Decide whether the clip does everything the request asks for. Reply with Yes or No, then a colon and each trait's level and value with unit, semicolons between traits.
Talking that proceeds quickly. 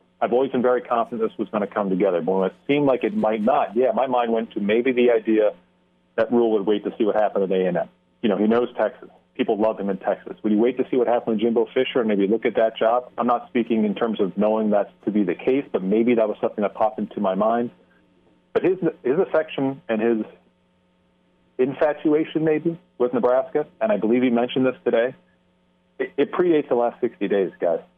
Yes: fast, 235 wpm